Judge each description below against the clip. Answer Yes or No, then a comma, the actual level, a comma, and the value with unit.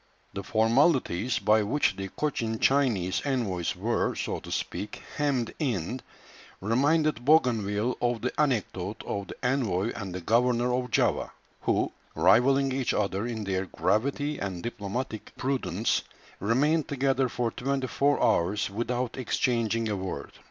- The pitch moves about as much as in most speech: Yes, average, 4.5 semitones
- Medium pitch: No, low, 120 Hz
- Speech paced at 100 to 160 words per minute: Yes, average, 140 wpm